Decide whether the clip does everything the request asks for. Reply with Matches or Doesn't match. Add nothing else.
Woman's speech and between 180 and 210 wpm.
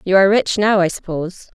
Doesn't match